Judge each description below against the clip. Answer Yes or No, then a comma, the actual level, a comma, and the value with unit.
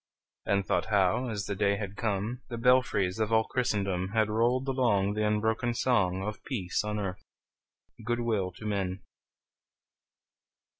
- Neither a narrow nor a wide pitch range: Yes, average, 3.0 semitones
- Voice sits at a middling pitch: No, low, 105 Hz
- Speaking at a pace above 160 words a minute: No, average, 150 wpm